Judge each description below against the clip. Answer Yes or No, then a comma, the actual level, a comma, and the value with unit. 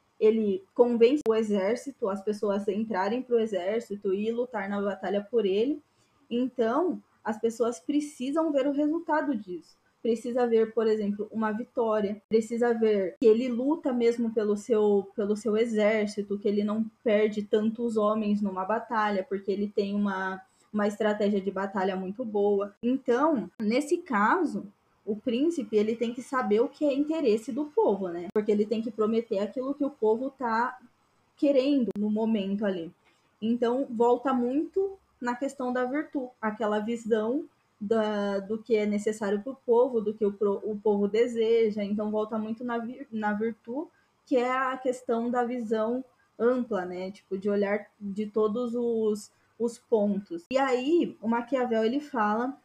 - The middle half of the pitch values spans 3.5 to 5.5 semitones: No, average, 3.1 semitones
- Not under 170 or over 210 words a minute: No, average, 160 wpm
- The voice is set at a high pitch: Yes, high, 225 Hz